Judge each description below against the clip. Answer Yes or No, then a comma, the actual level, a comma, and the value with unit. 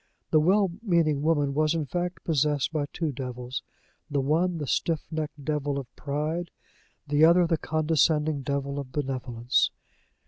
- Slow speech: No, average, 150 wpm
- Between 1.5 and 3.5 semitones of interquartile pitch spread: Yes, narrow, 2.6 semitones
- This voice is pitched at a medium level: Yes, medium, 150 Hz